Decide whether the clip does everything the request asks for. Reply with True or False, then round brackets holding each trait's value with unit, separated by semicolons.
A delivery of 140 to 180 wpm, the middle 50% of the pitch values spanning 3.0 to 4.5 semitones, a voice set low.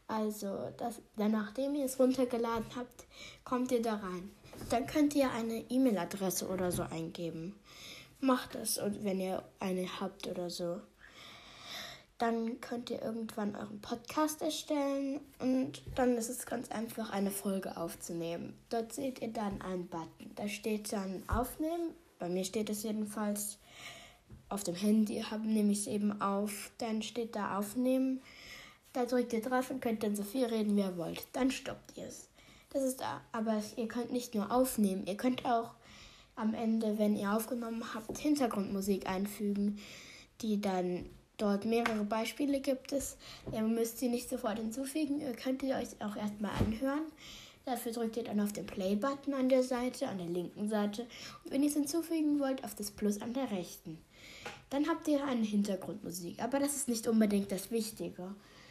False (170 wpm; 3.9 semitones; 225 Hz)